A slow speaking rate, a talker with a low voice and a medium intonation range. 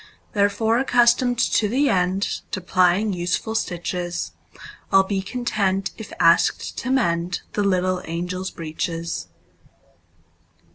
No: slow, 100 wpm; high, 190 Hz; average, 3.7 semitones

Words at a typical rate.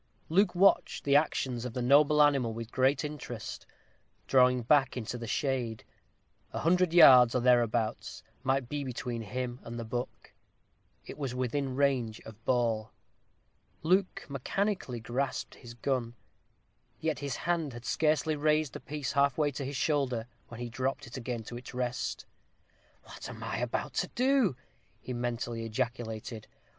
Yes: average, 155 wpm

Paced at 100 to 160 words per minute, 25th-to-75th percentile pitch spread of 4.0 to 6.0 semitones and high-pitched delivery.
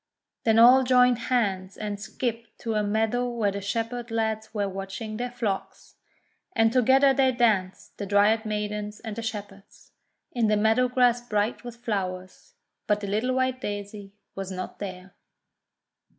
No: average, 155 wpm; average, 3.0 semitones; high, 220 Hz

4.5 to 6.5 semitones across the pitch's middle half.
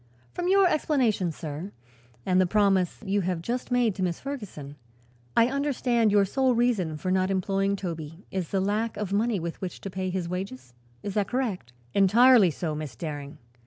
Yes: average, 4.9 semitones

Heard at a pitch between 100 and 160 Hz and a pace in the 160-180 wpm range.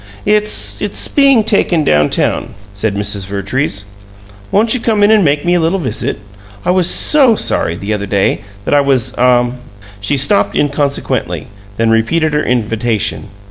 Yes: medium, 140 Hz; average, 170 wpm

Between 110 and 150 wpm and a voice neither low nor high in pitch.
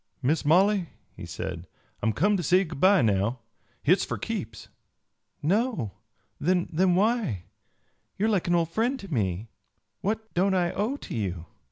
No: average, 160 wpm; medium, 175 Hz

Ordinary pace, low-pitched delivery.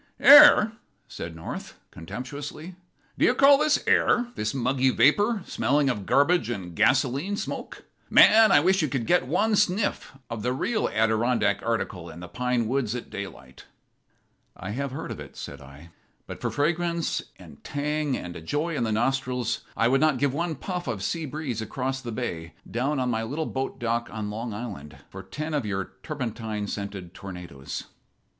Yes: average, 175 wpm; low, 125 Hz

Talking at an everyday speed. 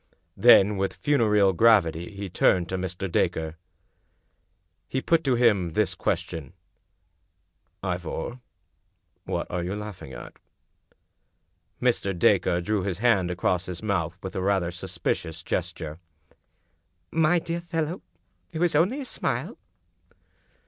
No: slow, 120 wpm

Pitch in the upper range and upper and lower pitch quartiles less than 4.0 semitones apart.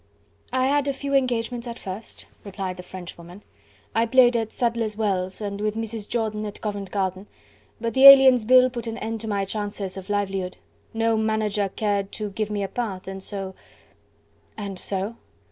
Yes: high, 215 Hz; average, 2.9 semitones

